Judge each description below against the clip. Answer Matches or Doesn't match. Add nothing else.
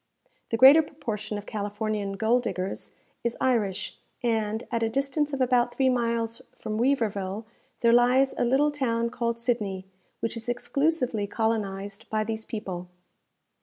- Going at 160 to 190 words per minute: Doesn't match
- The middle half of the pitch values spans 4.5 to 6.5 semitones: Doesn't match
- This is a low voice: Doesn't match